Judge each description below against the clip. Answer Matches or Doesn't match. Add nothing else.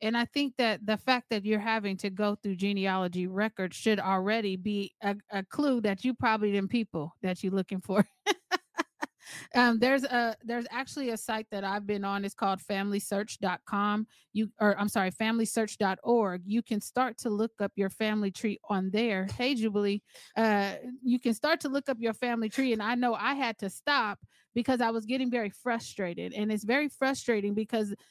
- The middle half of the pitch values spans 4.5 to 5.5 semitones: Doesn't match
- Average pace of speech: Matches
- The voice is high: Matches